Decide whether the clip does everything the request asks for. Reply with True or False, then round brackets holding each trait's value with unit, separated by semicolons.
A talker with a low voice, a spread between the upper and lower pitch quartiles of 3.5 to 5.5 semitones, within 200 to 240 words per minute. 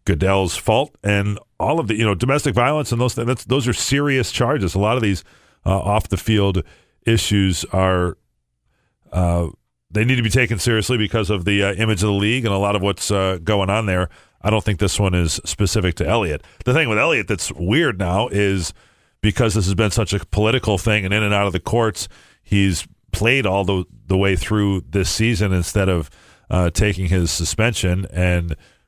False (100 Hz; 3.0 semitones; 205 wpm)